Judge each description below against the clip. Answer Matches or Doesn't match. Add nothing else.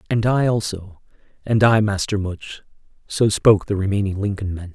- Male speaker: Matches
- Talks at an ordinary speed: Matches